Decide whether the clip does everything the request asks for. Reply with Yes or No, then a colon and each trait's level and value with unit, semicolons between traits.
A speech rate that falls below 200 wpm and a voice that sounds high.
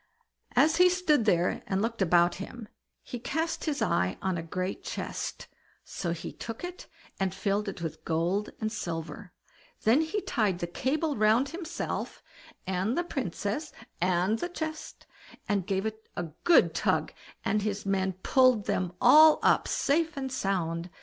Yes: average, 160 wpm; high, 215 Hz